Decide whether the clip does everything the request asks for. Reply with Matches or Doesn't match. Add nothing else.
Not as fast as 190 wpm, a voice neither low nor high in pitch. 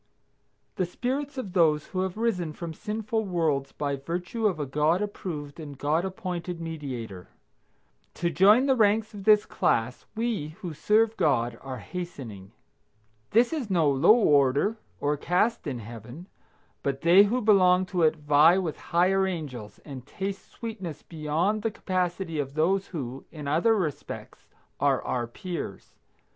Matches